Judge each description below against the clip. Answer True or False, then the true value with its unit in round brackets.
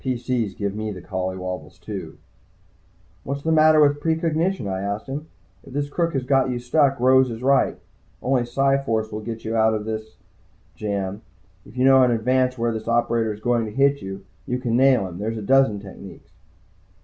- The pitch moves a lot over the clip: False (4.1 semitones)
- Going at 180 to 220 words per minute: True (195 wpm)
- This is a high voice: False (120 Hz)